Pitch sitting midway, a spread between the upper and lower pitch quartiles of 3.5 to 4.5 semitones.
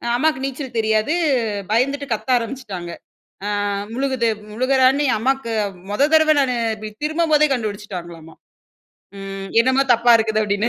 No: high, 240 Hz; average, 4.2 semitones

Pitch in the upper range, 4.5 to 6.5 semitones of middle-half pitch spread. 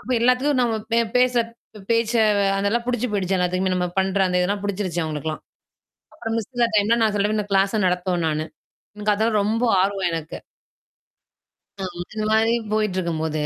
No: high, 205 Hz; average, 3.8 semitones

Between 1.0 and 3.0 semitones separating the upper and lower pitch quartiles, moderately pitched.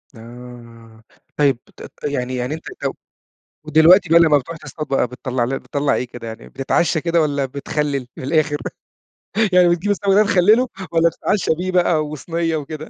No: average, 4.7 semitones; medium, 150 Hz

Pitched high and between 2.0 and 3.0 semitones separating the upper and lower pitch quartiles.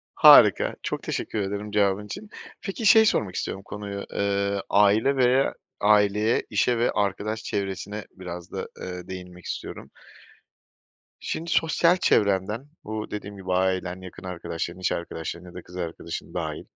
No: low, 100 Hz; narrow, 2.6 semitones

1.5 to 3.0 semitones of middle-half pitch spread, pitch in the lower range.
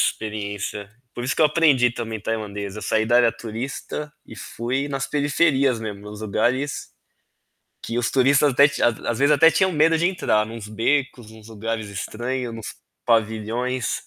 No: average, 4.2 semitones; low, 120 Hz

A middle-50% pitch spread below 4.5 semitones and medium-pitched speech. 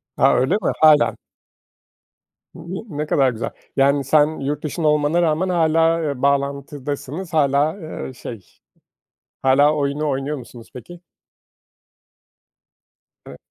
Yes: narrow, 2.5 semitones; medium, 150 Hz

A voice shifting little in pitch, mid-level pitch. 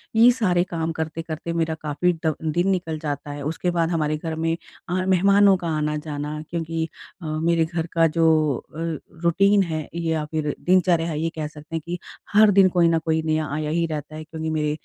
Yes: narrow, 1.8 semitones; medium, 160 Hz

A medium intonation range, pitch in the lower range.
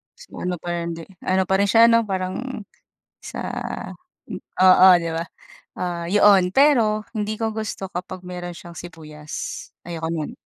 No: average, 3.7 semitones; medium, 185 Hz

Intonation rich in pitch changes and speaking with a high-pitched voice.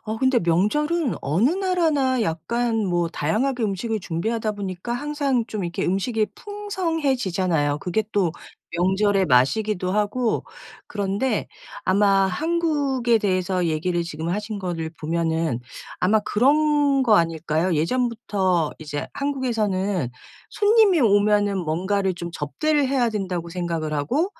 Yes: wide, 6.8 semitones; high, 205 Hz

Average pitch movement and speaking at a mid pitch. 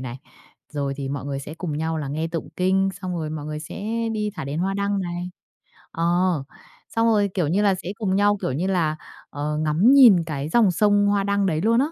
Yes: average, 4.9 semitones; medium, 175 Hz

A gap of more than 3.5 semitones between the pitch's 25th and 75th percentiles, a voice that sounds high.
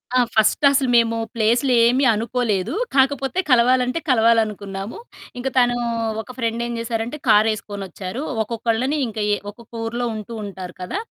No: average, 2.7 semitones; high, 230 Hz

